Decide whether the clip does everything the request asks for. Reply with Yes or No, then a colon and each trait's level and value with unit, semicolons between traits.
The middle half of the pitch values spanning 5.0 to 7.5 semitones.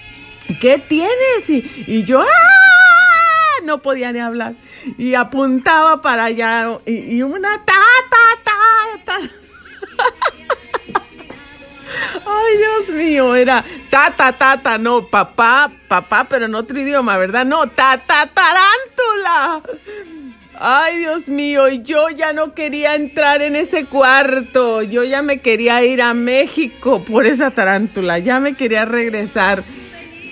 Yes: wide, 5.4 semitones